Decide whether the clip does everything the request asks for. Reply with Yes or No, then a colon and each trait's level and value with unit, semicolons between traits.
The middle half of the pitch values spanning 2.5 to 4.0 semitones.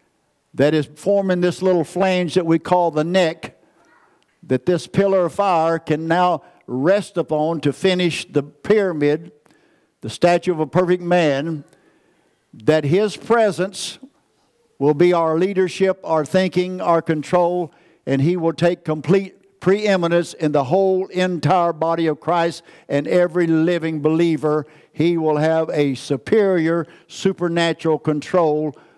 Yes: average, 2.8 semitones